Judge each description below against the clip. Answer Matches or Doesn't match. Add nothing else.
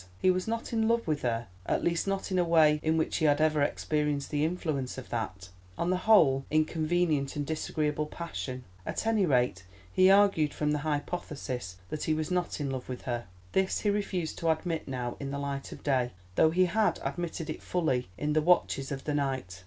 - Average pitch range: Matches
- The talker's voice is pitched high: Doesn't match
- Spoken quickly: Matches